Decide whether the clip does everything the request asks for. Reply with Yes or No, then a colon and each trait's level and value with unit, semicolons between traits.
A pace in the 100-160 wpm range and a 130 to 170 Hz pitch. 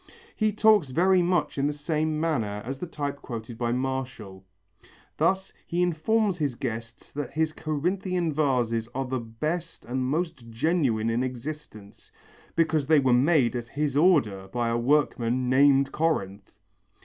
Yes: average, 150 wpm; medium, 140 Hz